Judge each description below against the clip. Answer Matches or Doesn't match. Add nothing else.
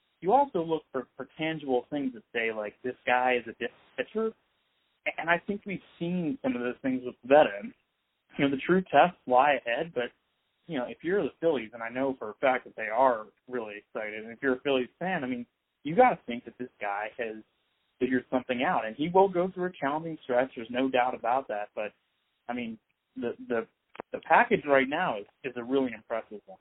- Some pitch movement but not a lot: Doesn't match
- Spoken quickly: Matches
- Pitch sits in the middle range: Doesn't match